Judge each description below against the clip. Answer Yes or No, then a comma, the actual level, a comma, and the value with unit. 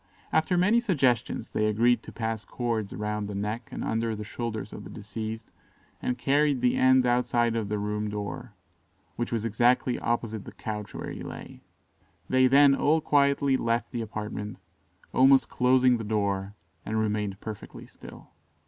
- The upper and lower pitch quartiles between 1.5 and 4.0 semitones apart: Yes, average, 3.2 semitones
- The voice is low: Yes, low, 115 Hz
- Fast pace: No, average, 160 wpm